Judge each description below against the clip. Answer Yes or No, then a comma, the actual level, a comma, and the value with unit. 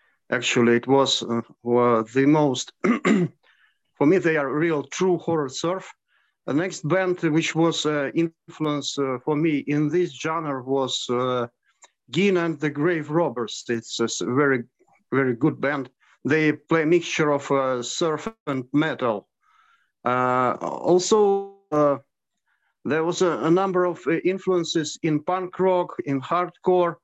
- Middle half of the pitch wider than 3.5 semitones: Yes, average, 4.4 semitones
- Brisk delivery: No, average, 150 wpm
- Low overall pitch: No, medium, 155 Hz